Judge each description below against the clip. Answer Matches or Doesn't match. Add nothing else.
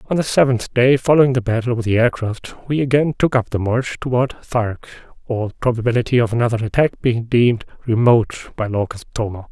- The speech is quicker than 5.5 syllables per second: Matches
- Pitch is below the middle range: Matches